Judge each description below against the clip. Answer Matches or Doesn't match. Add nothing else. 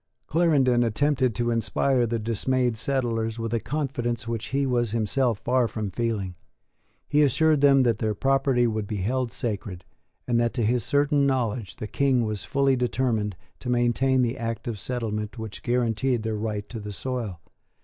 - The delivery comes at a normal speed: Matches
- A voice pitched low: Matches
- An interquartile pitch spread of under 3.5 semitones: Matches